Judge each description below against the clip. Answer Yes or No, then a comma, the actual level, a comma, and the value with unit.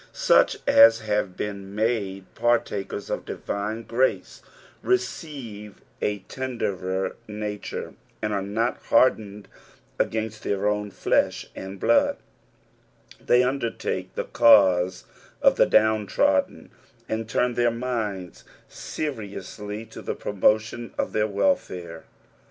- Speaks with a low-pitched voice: Yes, low, 105 Hz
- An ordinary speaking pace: No, slow, 110 wpm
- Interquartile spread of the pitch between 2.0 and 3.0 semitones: Yes, average, 2.7 semitones